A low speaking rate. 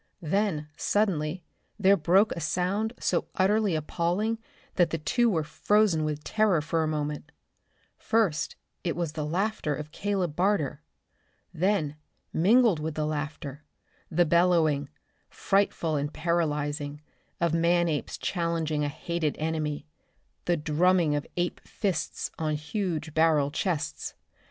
Yes: slow, 130 wpm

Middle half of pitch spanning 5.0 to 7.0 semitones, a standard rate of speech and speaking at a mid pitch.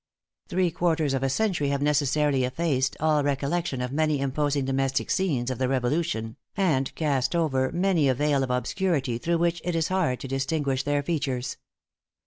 No: average, 3.7 semitones; average, 170 wpm; medium, 145 Hz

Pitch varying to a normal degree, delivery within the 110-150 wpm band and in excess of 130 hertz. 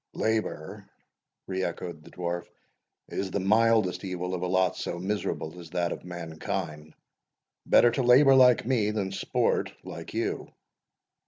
No: average, 3.9 semitones; average, 145 wpm; very low, 95 Hz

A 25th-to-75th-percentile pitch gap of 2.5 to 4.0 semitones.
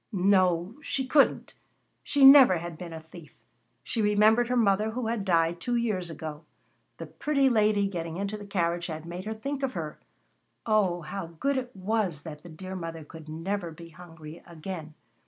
No: average, 4.9 semitones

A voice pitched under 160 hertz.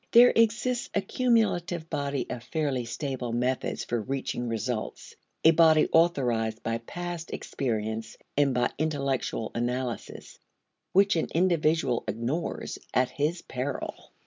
Yes: medium, 140 Hz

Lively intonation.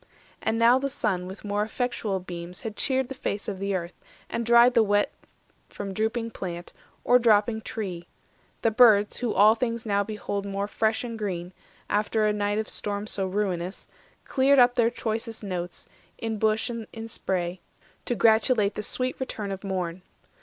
No: average, 2.8 semitones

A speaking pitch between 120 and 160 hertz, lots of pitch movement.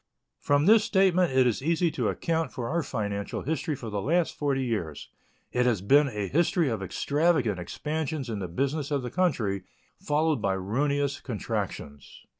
Yes: medium, 140 Hz; wide, 6.9 semitones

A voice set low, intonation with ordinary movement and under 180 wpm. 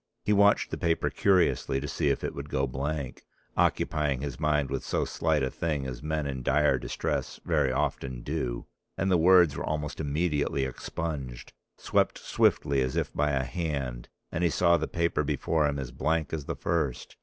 No: very low, 75 Hz; average, 3.2 semitones; average, 190 wpm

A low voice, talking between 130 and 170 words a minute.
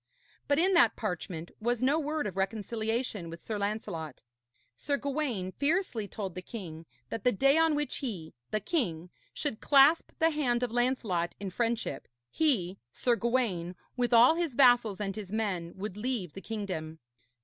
No: high, 225 Hz; average, 165 wpm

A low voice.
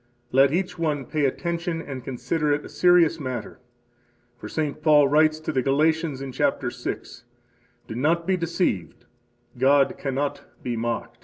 No: medium, 145 Hz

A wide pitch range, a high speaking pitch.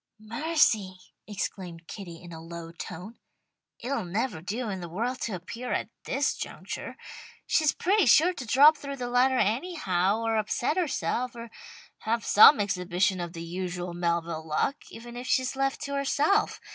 Yes: wide, 6.8 semitones; high, 220 Hz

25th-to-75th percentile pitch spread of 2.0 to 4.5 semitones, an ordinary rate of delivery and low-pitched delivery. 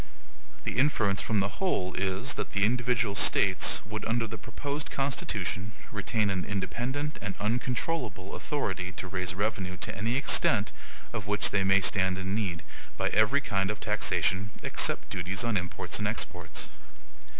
Yes: average, 3.8 semitones; average, 155 wpm; low, 100 Hz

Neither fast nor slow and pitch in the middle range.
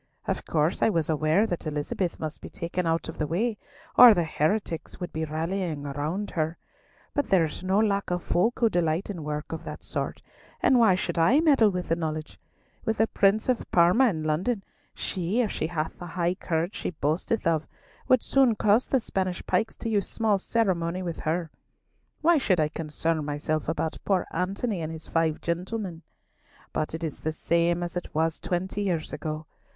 Yes: average, 195 wpm; medium, 175 Hz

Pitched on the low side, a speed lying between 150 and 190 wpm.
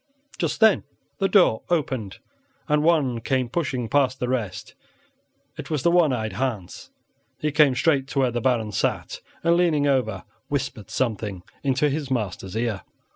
Yes: low, 130 Hz; average, 160 wpm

